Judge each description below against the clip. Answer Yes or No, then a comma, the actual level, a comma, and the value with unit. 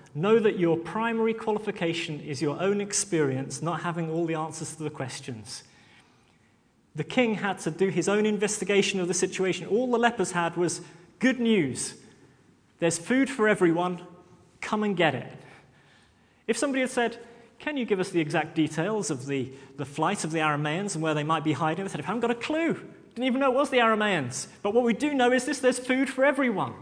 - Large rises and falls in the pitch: Yes, wide, 6.3 semitones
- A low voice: No, medium, 180 Hz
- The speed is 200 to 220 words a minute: Yes, fast, 205 wpm